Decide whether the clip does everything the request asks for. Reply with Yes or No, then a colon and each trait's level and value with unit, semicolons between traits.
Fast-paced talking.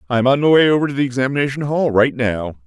Yes: fast, 250 wpm